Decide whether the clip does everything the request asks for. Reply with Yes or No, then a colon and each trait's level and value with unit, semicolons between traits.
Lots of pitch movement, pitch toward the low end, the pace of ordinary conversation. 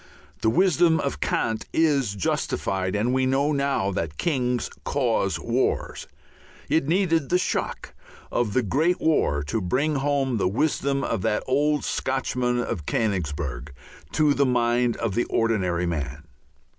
Yes: wide, 6.2 semitones; low, 125 Hz; average, 145 wpm